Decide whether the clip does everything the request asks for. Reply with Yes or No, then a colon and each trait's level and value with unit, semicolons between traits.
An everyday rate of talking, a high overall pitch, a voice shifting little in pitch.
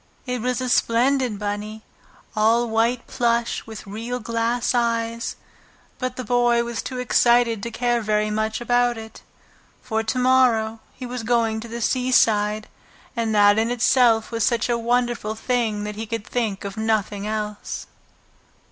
Yes: average, 155 wpm; high, 230 Hz; narrow, 1.9 semitones